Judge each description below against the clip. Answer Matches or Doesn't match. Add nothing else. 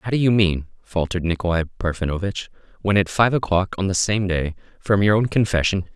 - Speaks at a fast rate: Doesn't match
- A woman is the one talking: Doesn't match